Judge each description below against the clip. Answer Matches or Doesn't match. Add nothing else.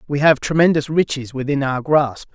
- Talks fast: Doesn't match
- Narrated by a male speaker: Matches